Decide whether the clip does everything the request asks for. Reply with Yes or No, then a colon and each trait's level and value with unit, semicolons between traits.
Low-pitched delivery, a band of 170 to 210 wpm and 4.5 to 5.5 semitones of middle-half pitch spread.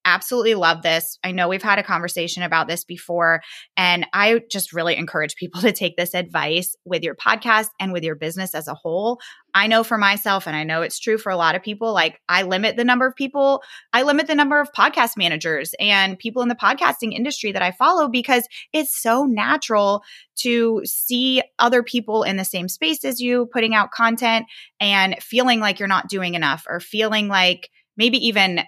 No: high, 200 Hz; fast, 205 wpm; average, 5.1 semitones